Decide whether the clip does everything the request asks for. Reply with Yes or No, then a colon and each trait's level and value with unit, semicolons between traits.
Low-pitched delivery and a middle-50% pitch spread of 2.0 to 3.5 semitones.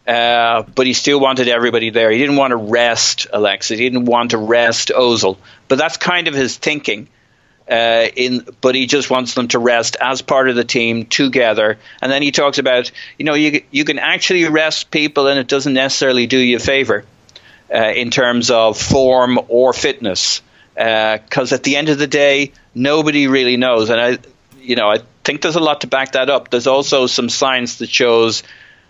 Yes: low, 130 Hz; average, 2.9 semitones